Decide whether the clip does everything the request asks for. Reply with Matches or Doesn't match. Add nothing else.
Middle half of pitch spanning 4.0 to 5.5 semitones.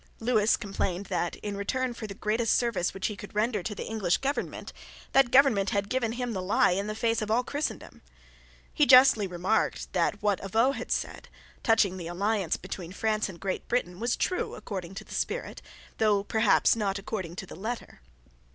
Doesn't match